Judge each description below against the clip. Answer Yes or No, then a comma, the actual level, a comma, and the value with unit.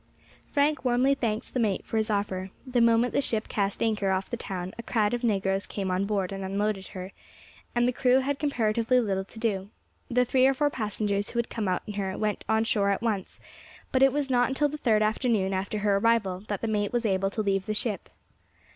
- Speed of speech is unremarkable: No, fast, 225 wpm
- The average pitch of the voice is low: No, high, 215 Hz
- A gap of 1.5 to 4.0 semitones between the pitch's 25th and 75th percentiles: Yes, average, 3.6 semitones